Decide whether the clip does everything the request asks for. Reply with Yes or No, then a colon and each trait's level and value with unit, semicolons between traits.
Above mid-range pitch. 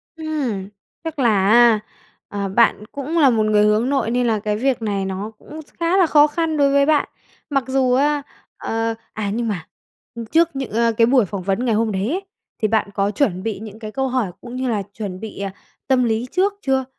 Yes: high, 235 Hz